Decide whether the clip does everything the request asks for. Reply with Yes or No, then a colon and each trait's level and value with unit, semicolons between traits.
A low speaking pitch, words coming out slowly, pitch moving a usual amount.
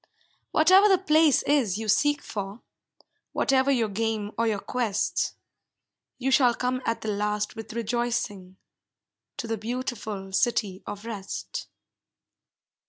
No: high, 230 Hz; slow, 125 wpm; average, 3.8 semitones